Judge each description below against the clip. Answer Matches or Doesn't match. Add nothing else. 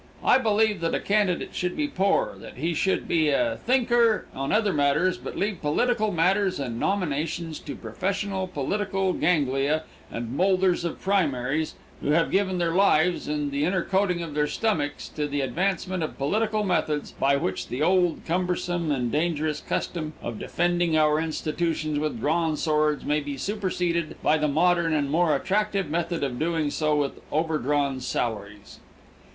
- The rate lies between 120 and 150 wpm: Doesn't match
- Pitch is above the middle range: Doesn't match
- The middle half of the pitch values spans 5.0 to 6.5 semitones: Doesn't match